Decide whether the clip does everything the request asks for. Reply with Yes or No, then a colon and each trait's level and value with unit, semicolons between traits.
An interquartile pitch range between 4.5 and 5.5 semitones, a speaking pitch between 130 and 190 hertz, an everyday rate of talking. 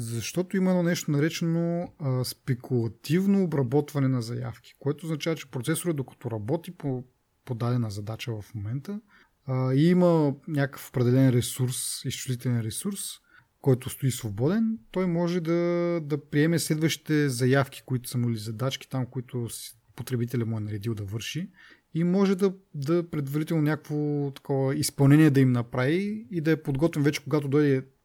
Yes: average, 4.8 semitones; medium, 140 Hz; average, 150 wpm